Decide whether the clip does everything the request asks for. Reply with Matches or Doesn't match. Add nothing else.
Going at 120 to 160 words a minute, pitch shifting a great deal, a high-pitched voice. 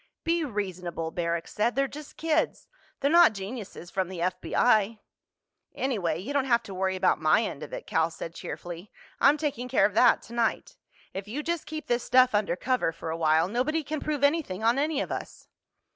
Doesn't match